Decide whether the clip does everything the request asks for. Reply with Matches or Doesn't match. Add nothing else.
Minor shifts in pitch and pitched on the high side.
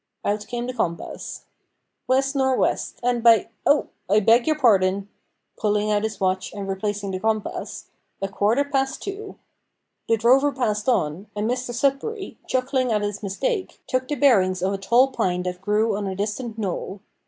Doesn't match